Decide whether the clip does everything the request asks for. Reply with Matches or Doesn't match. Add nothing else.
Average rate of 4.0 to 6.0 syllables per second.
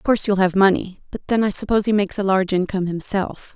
Doesn't match